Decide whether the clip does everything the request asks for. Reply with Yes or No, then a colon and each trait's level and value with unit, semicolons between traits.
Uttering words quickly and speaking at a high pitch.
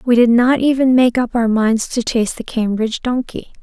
Yes: fast, 215 wpm; high, 240 Hz